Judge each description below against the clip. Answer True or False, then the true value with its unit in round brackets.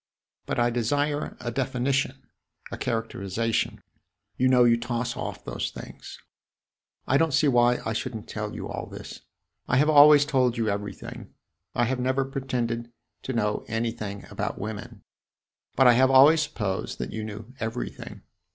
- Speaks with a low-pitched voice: True (120 Hz)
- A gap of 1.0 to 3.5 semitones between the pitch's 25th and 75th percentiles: True (2.9 semitones)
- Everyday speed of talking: True (160 wpm)